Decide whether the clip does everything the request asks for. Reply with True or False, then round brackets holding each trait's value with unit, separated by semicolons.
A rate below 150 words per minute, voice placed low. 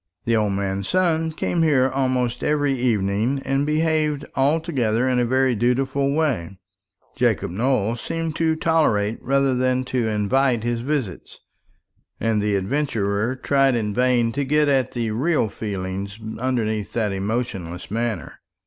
True (140 wpm; 125 Hz)